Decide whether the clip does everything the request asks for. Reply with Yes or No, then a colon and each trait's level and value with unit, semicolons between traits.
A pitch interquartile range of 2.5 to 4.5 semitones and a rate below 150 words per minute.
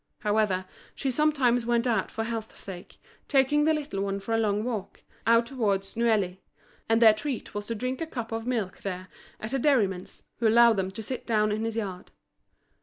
No: average, 3.2 semitones; average, 195 wpm